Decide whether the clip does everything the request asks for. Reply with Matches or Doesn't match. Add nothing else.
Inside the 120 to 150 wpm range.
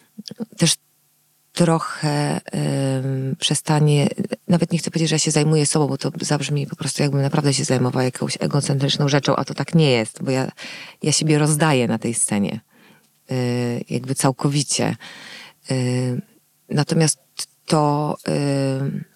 Matches